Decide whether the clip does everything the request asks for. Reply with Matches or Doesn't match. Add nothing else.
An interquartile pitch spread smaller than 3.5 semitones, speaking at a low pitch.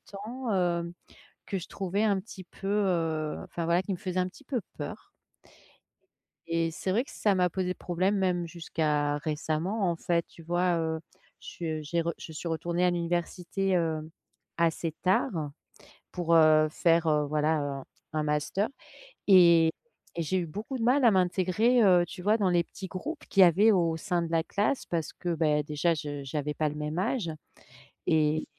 Doesn't match